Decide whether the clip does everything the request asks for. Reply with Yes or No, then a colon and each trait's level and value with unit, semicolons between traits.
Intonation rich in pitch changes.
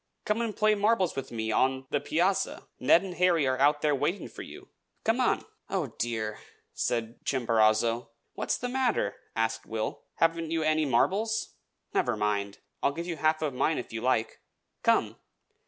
Yes: wide, 7.9 semitones